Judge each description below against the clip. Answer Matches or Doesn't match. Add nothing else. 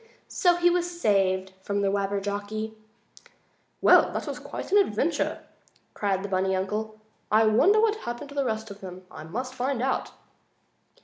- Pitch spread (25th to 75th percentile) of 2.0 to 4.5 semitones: Doesn't match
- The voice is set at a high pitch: Matches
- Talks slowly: Doesn't match